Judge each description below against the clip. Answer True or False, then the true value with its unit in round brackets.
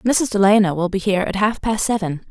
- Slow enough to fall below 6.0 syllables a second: True (5.8 syllables/s)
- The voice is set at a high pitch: True (200 Hz)